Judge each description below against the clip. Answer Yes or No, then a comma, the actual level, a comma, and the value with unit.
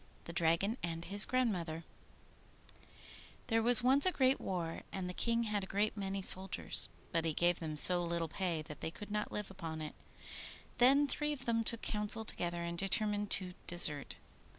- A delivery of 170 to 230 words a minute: Yes, average, 180 wpm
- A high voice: Yes, high, 195 Hz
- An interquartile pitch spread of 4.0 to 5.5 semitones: Yes, average, 4.8 semitones